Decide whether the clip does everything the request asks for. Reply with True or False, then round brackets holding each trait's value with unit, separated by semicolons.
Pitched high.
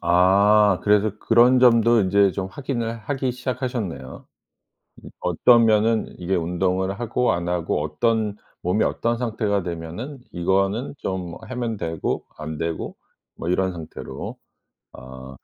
False (100 Hz)